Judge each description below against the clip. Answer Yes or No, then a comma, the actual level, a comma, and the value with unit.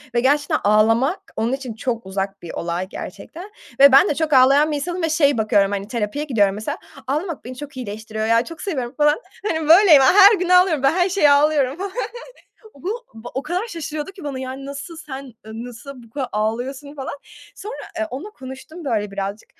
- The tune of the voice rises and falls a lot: Yes, wide, 5.7 semitones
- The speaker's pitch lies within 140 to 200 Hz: No, very high, 275 Hz